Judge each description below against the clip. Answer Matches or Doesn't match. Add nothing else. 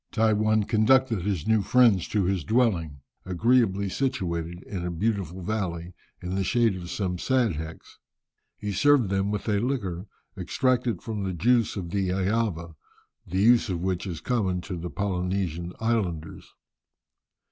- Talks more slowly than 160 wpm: Matches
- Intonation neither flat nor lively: Matches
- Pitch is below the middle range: Matches